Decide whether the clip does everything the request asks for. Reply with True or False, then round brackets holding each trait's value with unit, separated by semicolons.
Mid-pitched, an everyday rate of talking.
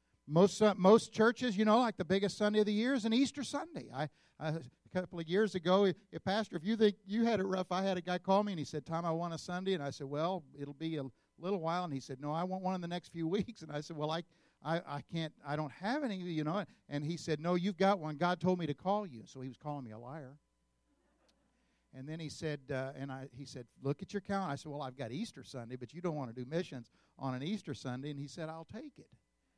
False (165 Hz; 285 wpm)